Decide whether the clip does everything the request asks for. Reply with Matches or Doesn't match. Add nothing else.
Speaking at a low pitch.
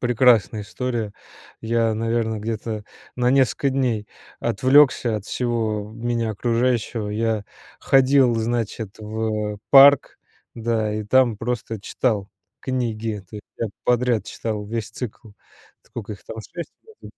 Matches